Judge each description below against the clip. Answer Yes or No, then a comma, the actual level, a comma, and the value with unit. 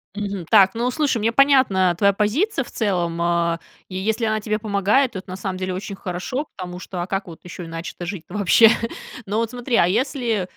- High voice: Yes, high, 200 Hz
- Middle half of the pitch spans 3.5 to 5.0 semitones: Yes, average, 4.1 semitones